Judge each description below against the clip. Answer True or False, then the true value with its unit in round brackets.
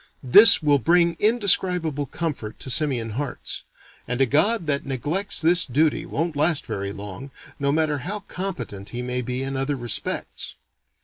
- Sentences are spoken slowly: False (160 wpm)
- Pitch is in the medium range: True (145 Hz)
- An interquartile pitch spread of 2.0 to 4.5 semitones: False (5.2 semitones)